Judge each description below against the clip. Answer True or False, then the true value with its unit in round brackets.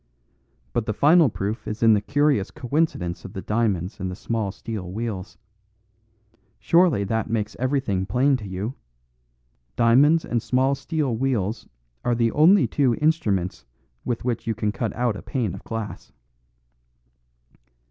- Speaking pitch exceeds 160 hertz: False (115 Hz)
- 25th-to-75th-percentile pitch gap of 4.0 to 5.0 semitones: True (4.6 semitones)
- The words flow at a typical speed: True (145 wpm)